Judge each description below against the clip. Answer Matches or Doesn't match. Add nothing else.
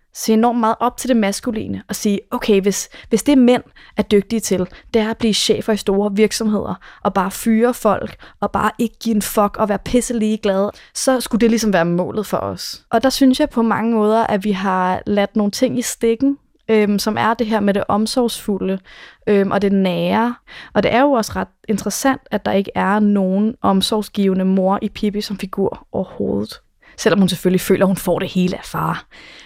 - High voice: Matches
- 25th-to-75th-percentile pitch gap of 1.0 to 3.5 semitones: Matches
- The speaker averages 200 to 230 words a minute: Matches